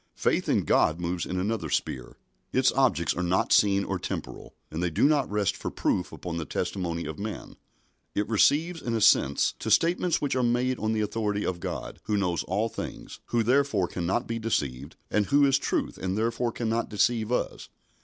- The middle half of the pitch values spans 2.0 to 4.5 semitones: No, average, 5.2 semitones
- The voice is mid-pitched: No, low, 105 Hz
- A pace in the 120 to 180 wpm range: No, average, 195 wpm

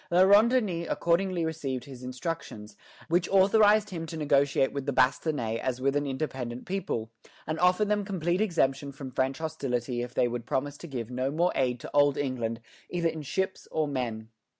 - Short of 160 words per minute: No, average, 185 wpm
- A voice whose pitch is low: No, medium, 145 Hz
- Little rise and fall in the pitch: No, average, 5.2 semitones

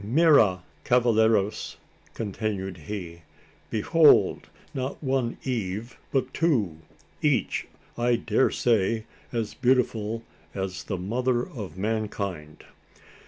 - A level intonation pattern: No, average, 4.2 semitones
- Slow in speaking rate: Yes, slow, 90 wpm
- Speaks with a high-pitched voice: No, low, 110 Hz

